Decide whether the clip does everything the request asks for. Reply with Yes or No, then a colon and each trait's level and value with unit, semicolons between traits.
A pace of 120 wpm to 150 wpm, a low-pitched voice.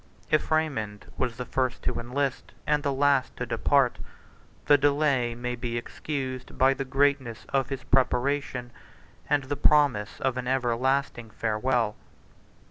Yes: average, 140 wpm; low, 130 Hz